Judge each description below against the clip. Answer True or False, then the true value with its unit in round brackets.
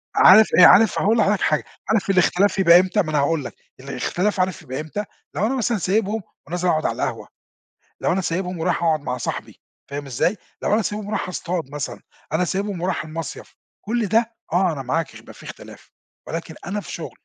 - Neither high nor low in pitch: True (180 Hz)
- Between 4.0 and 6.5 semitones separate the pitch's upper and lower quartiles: True (4.4 semitones)